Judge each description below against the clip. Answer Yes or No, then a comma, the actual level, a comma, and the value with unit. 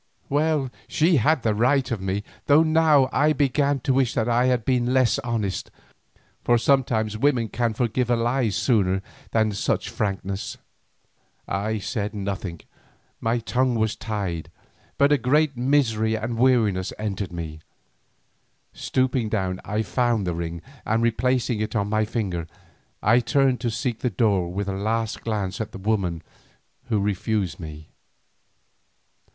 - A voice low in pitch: Yes, low, 115 Hz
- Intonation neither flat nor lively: Yes, average, 4.1 semitones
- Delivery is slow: No, average, 150 wpm